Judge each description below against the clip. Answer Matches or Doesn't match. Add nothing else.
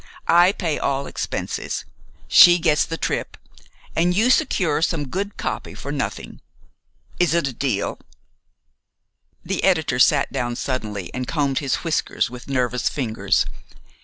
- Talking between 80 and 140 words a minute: Matches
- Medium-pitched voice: Matches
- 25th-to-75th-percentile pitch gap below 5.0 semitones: Doesn't match